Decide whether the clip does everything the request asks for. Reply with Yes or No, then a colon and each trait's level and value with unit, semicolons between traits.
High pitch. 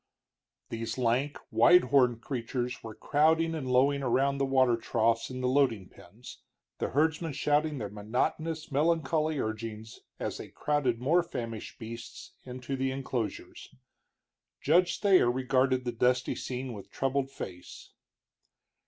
No: low, 130 Hz